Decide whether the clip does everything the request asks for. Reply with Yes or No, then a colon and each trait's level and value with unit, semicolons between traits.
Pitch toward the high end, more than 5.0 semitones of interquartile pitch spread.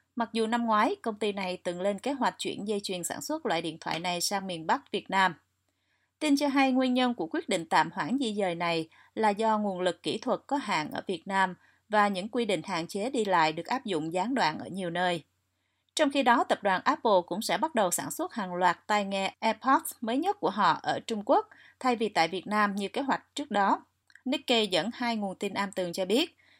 Yes: high, 210 Hz; wide, 5.6 semitones